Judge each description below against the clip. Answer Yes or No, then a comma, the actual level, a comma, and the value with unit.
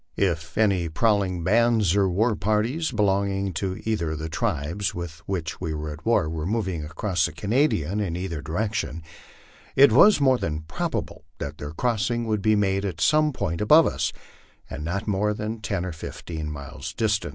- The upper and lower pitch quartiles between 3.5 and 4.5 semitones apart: No, average, 5.0 semitones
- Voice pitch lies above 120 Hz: No, very low, 95 Hz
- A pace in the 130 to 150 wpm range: No, average, 180 wpm